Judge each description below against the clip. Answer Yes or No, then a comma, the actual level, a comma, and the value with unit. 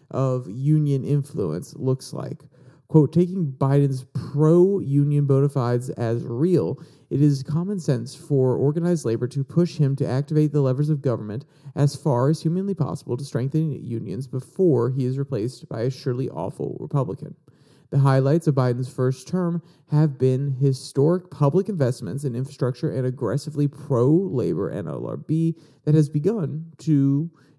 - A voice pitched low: No, medium, 145 Hz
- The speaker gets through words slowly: No, average, 150 wpm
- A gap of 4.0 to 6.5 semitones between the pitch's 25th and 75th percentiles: No, average, 2.9 semitones